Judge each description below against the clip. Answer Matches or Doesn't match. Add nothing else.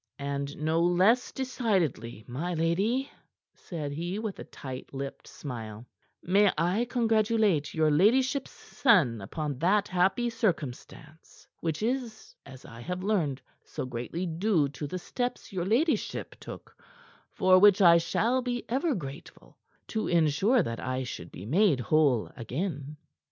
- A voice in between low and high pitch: Matches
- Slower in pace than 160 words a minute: Matches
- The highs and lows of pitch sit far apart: Matches